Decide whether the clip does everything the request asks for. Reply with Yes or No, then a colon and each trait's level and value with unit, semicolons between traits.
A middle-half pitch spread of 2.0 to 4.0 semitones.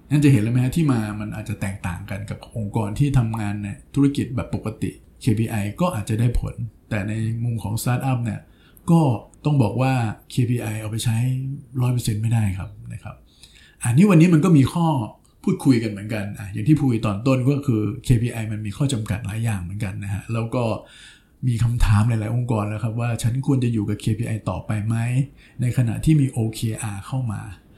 Yes: average, 3.3 semitones